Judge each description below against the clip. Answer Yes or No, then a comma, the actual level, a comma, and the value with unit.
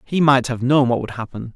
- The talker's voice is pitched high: No, low, 125 Hz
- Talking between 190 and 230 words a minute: No, fast, 270 wpm